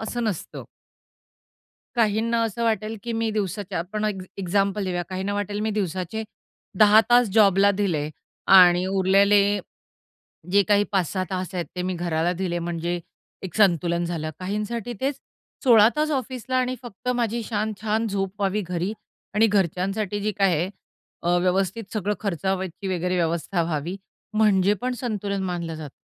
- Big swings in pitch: No, average, 3.2 semitones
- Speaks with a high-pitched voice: Yes, high, 195 Hz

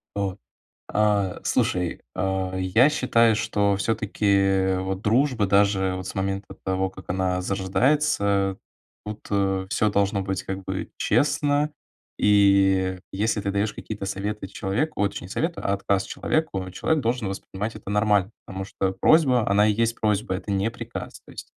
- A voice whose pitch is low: Yes, low, 100 Hz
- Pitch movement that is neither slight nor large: No, narrow, 2.2 semitones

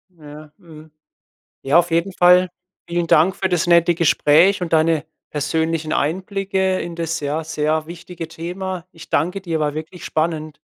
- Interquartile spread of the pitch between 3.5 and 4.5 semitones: No, narrow, 2.4 semitones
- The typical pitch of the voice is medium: Yes, medium, 165 Hz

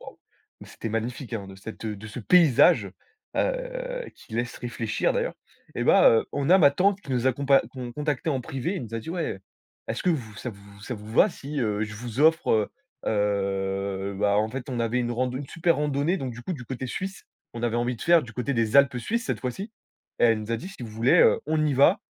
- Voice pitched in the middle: No, low, 125 Hz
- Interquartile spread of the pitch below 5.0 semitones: No, average, 5.3 semitones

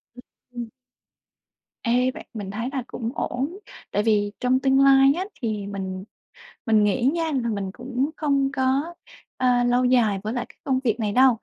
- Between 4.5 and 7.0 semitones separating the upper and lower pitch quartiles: No, average, 3.7 semitones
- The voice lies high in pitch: Yes, high, 245 Hz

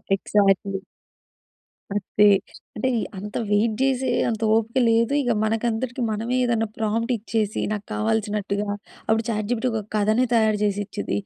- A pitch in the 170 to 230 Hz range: Yes, high, 220 Hz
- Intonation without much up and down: Yes, narrow, 1.8 semitones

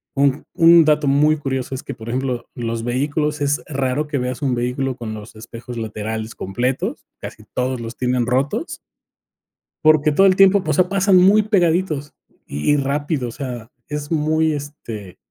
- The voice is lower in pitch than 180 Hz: Yes, medium, 140 Hz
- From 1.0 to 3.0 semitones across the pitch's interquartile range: No, average, 4.0 semitones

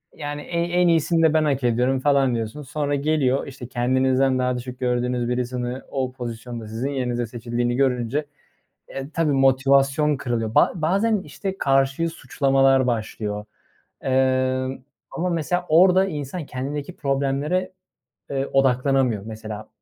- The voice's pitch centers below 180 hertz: Yes, low, 135 Hz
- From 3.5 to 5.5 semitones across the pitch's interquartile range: No, average, 3.1 semitones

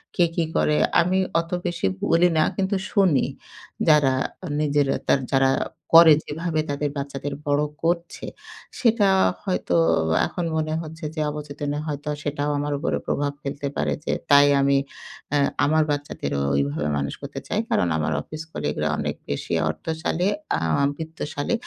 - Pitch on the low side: No, medium, 150 Hz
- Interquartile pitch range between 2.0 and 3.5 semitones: Yes, average, 2.8 semitones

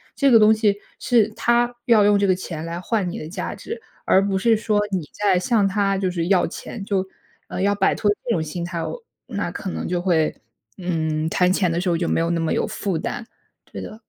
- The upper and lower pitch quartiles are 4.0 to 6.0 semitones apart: No, average, 3.5 semitones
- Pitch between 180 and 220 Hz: Yes, high, 190 Hz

